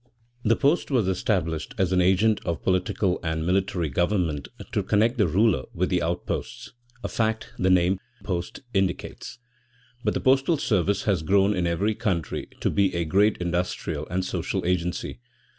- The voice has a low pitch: Yes, very low, 95 Hz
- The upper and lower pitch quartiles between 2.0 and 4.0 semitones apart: Yes, average, 3.4 semitones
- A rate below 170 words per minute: Yes, average, 160 wpm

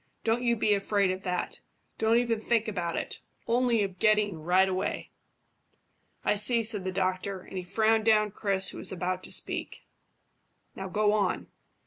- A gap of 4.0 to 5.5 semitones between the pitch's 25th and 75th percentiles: No, average, 3.0 semitones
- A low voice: No, high, 205 Hz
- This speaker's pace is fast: No, average, 170 wpm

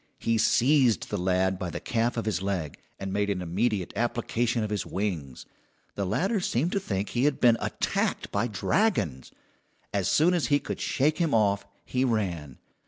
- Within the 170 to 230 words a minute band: Yes, average, 180 wpm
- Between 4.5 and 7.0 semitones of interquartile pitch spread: Yes, average, 4.8 semitones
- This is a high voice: No, low, 110 Hz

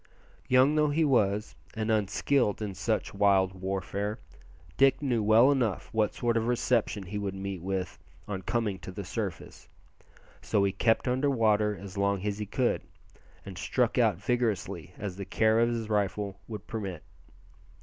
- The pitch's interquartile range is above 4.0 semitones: No, average, 3.2 semitones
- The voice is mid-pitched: No, low, 105 Hz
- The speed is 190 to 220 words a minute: No, average, 170 wpm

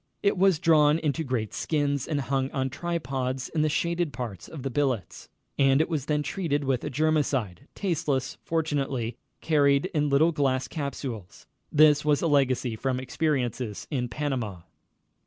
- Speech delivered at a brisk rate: No, average, 155 wpm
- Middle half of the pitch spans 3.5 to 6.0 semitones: No, average, 3.1 semitones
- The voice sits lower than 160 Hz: Yes, medium, 140 Hz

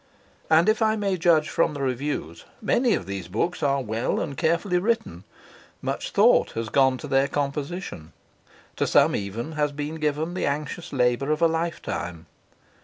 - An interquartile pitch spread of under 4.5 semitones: No, average, 5.2 semitones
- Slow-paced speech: No, average, 170 wpm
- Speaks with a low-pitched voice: No, medium, 145 Hz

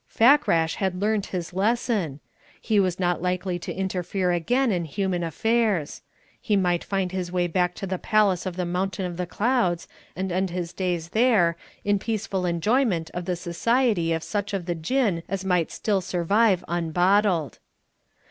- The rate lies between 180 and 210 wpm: No, average, 165 wpm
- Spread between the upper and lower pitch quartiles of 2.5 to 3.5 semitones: Yes, average, 2.9 semitones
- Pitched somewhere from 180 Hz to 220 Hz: Yes, medium, 185 Hz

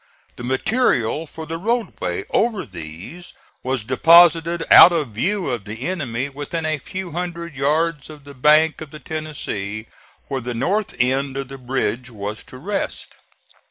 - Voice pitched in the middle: Yes, medium, 145 Hz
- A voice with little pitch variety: No, average, 5.2 semitones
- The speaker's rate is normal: Yes, average, 160 wpm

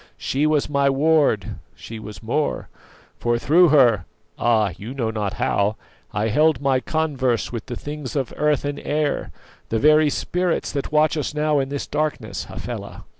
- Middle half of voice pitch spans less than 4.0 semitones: No, average, 4.7 semitones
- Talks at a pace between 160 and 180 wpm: Yes, average, 170 wpm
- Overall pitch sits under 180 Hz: Yes, medium, 140 Hz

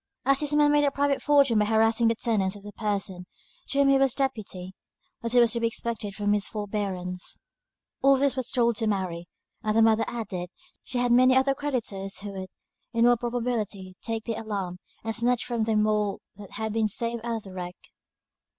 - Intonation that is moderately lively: Yes, average, 3.2 semitones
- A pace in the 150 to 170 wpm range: No, fast, 205 wpm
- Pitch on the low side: No, high, 225 Hz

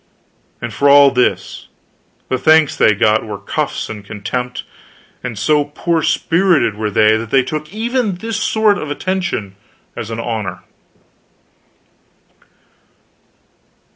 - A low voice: Yes, low, 130 Hz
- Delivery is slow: Yes, slow, 125 wpm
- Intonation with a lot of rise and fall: Yes, wide, 7.2 semitones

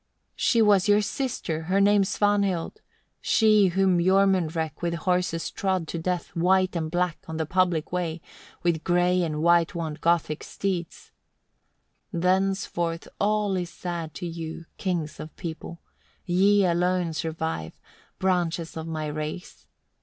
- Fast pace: No, average, 145 wpm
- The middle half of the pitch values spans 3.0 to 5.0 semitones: No, narrow, 2.5 semitones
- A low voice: No, medium, 175 Hz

